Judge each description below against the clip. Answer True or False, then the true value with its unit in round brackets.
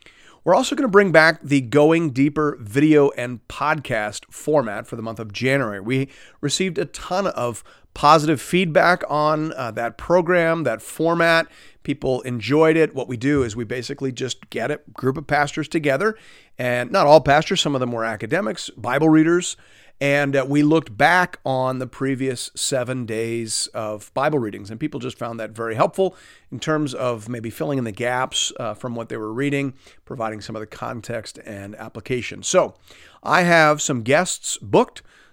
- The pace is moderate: True (180 wpm)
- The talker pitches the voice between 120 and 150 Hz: True (135 Hz)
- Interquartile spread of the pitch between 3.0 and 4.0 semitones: False (4.7 semitones)